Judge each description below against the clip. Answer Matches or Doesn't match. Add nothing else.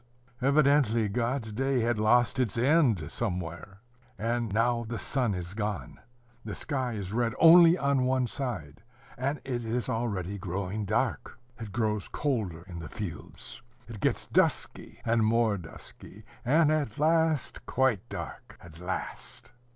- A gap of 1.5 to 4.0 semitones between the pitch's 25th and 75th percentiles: Doesn't match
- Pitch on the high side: Doesn't match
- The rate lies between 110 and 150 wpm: Matches